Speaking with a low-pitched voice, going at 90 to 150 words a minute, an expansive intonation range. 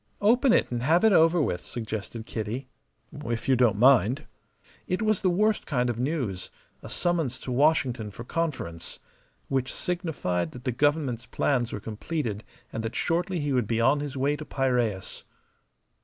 No: low, 130 Hz; average, 170 wpm; wide, 5.9 semitones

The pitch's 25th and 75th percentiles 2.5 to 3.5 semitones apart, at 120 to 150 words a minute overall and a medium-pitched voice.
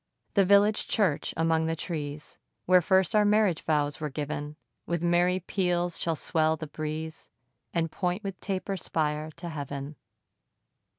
Yes: average, 3.2 semitones; average, 145 wpm; medium, 165 Hz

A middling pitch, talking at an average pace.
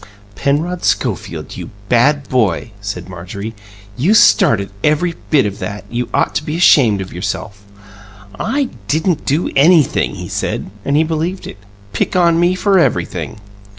Yes: medium, 145 Hz; average, 150 wpm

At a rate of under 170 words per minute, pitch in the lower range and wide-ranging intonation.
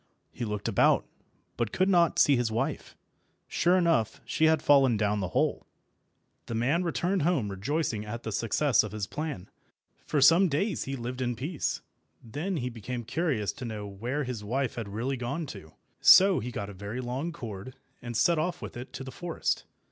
No: average, 190 wpm; low, 125 Hz; wide, 6.3 semitones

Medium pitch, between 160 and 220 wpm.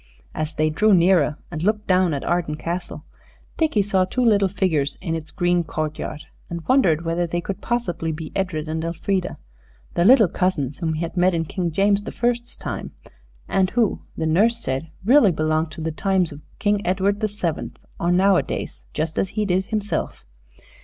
Yes: medium, 180 Hz; average, 185 wpm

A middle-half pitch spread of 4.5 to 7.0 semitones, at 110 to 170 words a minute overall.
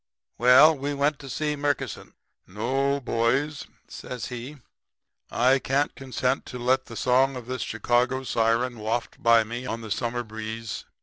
No: average, 2.7 semitones; average, 150 wpm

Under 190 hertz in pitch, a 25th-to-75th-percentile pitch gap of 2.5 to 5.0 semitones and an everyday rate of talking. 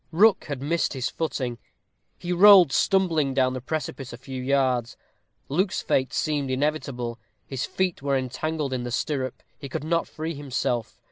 Yes: medium, 140 Hz; average, 3.7 semitones; average, 160 wpm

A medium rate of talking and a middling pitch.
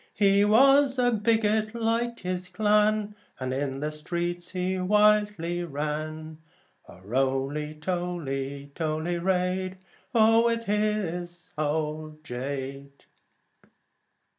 No: slow, 95 wpm; medium, 175 Hz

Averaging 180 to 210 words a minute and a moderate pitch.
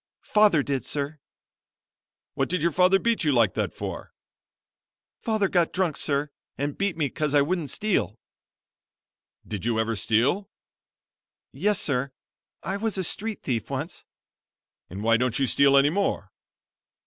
No: average, 150 wpm; medium, 150 Hz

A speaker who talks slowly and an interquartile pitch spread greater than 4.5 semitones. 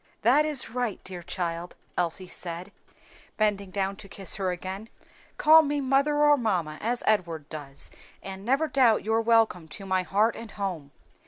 No: average, 165 wpm; average, 5.0 semitones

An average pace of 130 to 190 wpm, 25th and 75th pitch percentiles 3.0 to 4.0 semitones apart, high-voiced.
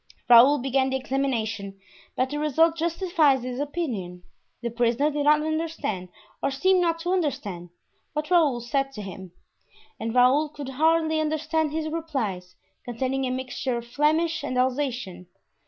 No: average, 150 wpm; average, 4.6 semitones; very high, 270 Hz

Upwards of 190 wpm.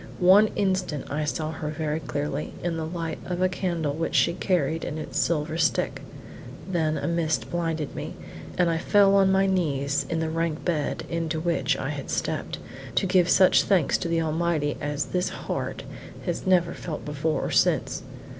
No: average, 185 wpm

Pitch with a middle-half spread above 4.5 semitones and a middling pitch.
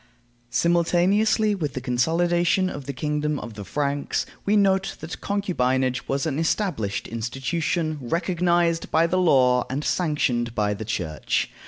Yes: wide, 5.6 semitones; medium, 150 Hz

